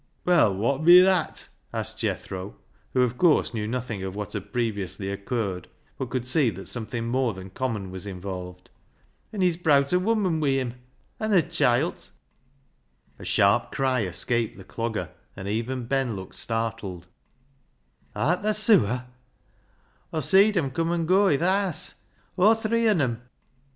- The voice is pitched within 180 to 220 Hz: No, low, 125 Hz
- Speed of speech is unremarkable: Yes, average, 165 wpm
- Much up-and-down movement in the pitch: Yes, wide, 8.5 semitones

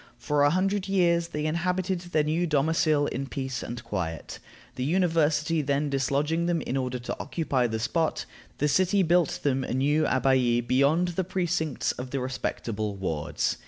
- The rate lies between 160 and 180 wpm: Yes, average, 165 wpm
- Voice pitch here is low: No, medium, 150 Hz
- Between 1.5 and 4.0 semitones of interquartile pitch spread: No, average, 4.6 semitones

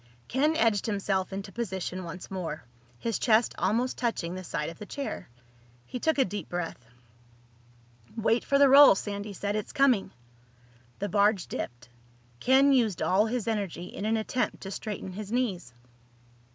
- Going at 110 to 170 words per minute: Yes, average, 160 wpm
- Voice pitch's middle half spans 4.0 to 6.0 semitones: Yes, average, 4.3 semitones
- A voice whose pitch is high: Yes, high, 205 Hz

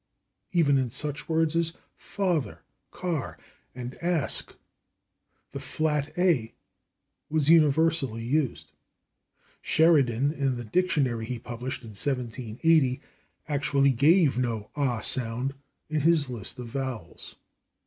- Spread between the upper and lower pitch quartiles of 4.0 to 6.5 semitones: Yes, average, 4.5 semitones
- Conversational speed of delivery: No, slow, 110 wpm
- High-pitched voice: No, medium, 140 Hz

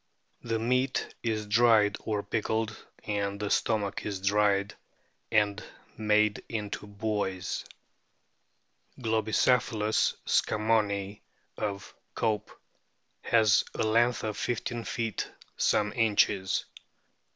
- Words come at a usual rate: No, slow, 95 wpm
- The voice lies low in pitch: Yes, low, 105 Hz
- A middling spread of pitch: No, narrow, 1.7 semitones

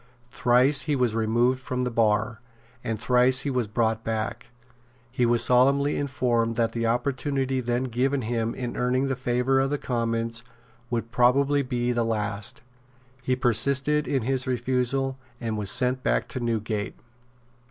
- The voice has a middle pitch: No, low, 125 Hz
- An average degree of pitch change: No, narrow, 2.2 semitones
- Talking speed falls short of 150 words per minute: No, average, 155 wpm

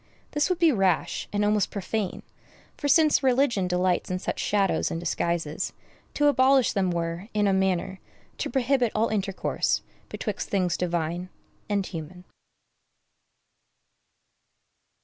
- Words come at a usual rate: No, slow, 130 wpm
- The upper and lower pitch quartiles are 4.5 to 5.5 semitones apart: Yes, average, 5.2 semitones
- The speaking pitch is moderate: No, high, 195 Hz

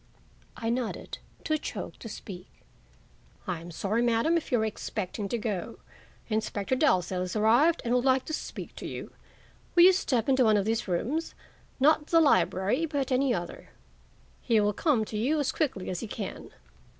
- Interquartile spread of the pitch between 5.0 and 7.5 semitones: Yes, average, 5.3 semitones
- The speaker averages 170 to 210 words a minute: Yes, average, 180 wpm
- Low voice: No, high, 230 Hz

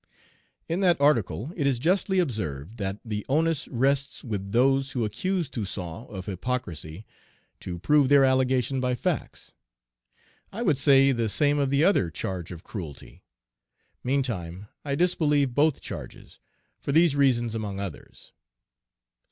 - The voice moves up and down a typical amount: No, wide, 6.0 semitones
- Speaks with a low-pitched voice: Yes, low, 130 Hz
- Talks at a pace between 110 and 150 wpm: Yes, average, 140 wpm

